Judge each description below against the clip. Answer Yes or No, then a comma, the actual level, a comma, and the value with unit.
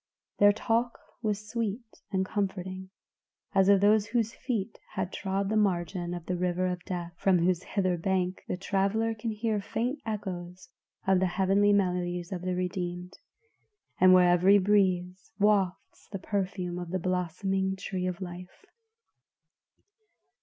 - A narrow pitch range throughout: Yes, narrow, 2.2 semitones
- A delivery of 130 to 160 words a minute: Yes, average, 145 wpm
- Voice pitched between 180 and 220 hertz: Yes, high, 190 Hz